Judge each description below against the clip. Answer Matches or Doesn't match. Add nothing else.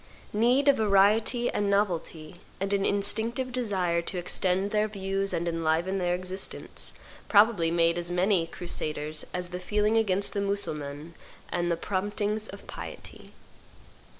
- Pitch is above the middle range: Matches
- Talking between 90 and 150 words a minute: Matches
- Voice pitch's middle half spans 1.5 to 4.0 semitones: Matches